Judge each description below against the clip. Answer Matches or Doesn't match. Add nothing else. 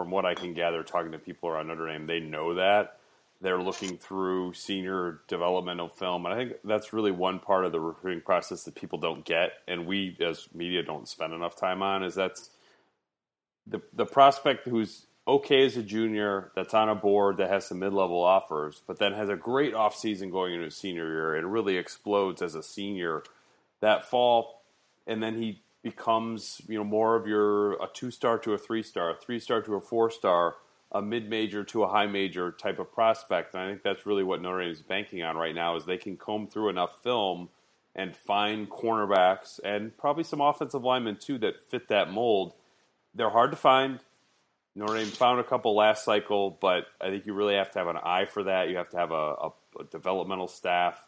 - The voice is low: Matches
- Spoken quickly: Matches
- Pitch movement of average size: Matches